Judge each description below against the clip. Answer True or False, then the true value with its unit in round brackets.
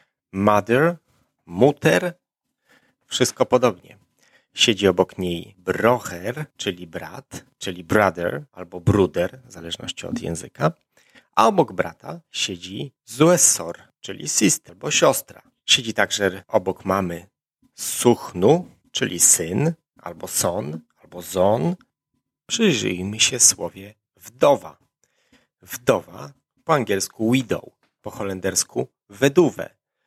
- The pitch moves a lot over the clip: True (6.0 semitones)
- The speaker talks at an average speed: False (100 wpm)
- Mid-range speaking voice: False (105 Hz)